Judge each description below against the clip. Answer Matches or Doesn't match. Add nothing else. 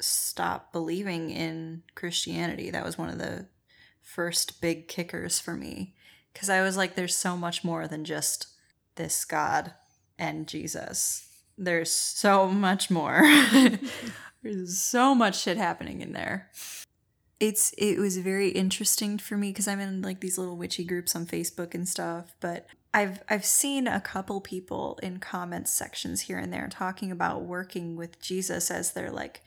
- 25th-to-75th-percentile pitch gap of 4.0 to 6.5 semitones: Doesn't match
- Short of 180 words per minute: Matches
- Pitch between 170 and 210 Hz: Matches